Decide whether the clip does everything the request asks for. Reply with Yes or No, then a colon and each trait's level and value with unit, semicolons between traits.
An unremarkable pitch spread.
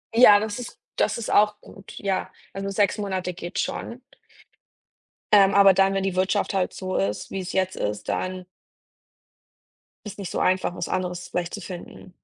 No: narrow, 1.7 semitones